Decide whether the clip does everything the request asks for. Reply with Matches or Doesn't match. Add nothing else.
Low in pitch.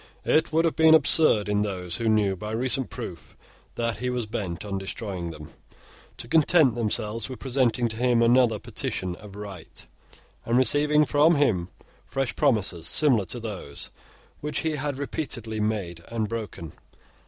Matches